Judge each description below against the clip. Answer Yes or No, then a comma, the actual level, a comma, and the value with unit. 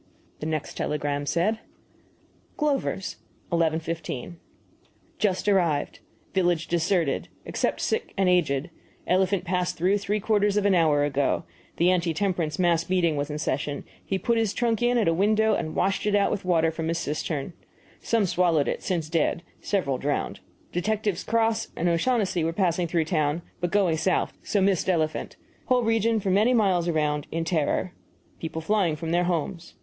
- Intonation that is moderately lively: Yes, average, 3.9 semitones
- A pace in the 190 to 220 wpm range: No, average, 165 wpm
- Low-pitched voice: No, medium, 175 Hz